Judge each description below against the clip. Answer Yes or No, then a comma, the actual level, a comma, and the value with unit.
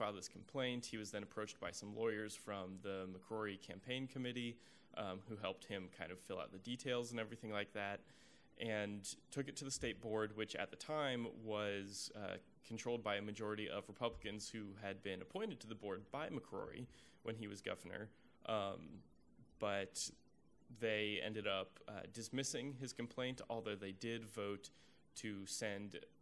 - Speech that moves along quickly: No, average, 175 wpm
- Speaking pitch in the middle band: No, low, 105 Hz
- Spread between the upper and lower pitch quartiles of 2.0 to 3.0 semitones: Yes, average, 2.7 semitones